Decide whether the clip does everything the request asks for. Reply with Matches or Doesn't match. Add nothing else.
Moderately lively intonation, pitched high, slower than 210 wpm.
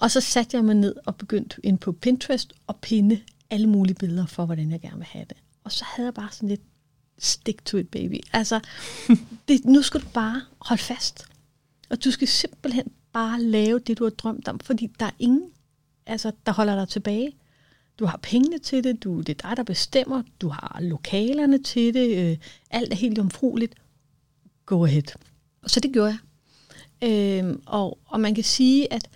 Matches